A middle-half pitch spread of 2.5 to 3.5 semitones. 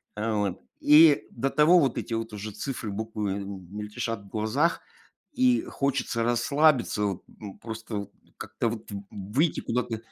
No: average, 4.6 semitones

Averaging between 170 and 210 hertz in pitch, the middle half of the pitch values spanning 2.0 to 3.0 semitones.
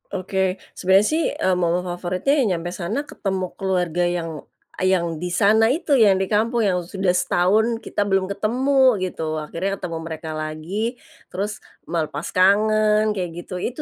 No: high, 190 Hz; average, 3.6 semitones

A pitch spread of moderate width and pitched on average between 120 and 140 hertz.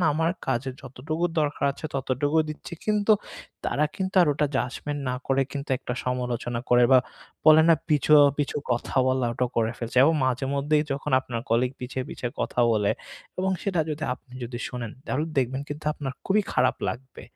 Yes: average, 3.5 semitones; low, 135 Hz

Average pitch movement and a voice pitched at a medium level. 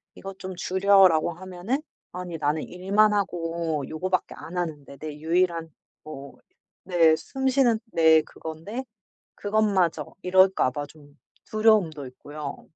Yes: average, 3.7 semitones; medium, 175 Hz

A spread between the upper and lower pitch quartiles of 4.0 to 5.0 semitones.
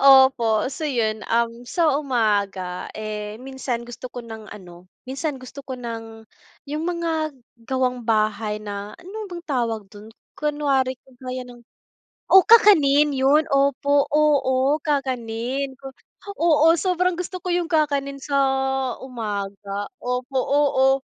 Yes: average, 4.6 semitones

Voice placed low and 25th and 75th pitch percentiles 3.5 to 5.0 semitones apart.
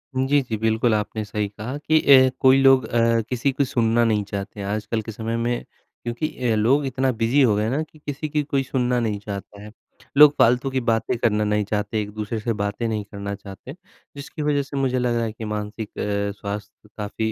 Yes: low, 115 Hz; average, 3.8 semitones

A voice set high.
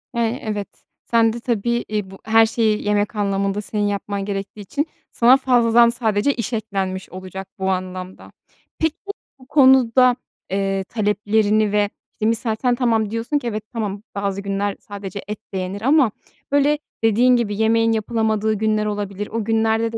Yes: high, 215 Hz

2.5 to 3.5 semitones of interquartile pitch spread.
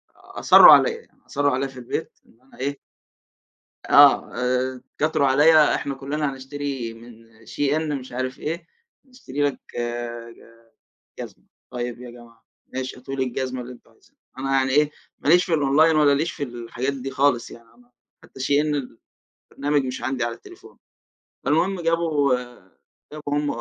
Yes: average, 2.8 semitones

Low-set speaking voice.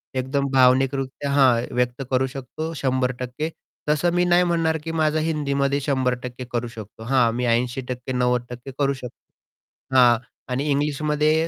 Yes: low, 130 Hz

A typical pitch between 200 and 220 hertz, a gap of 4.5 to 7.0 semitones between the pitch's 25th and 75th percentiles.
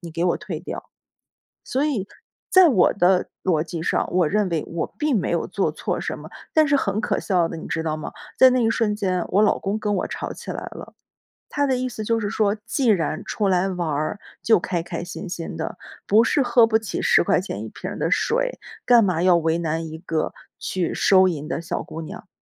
No: high, 190 Hz; average, 5.0 semitones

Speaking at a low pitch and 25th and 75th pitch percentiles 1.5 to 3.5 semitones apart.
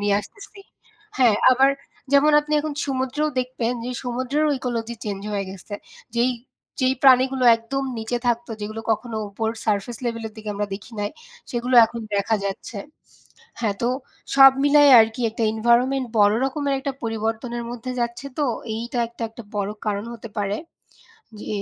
No: high, 235 Hz; average, 3.0 semitones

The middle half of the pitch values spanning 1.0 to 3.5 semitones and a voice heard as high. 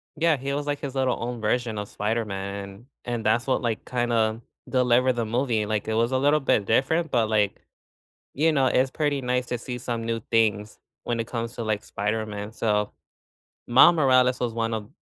No: average, 3.0 semitones; low, 120 Hz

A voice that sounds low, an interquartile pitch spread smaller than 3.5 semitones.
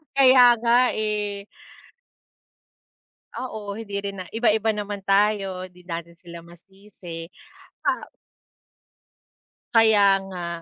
No: high, 200 Hz; average, 3.0 semitones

